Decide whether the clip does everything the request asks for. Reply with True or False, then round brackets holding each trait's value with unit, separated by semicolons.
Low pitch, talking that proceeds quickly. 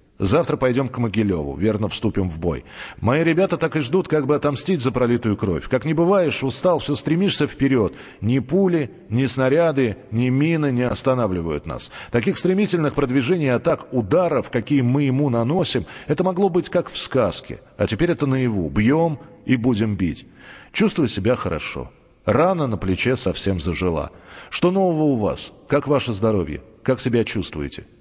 True (130 Hz; 165 wpm)